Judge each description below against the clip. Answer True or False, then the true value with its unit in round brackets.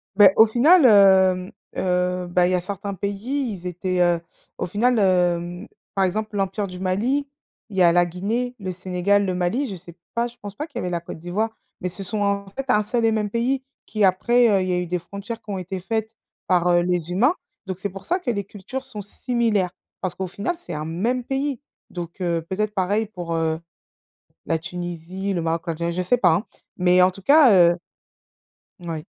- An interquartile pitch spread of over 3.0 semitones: True (3.6 semitones)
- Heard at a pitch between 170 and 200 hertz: True (190 Hz)